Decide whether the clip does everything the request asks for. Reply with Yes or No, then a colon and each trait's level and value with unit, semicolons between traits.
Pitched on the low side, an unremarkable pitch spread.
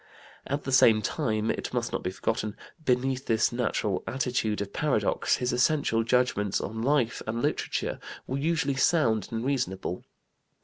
Yes: low, 120 Hz; average, 3.6 semitones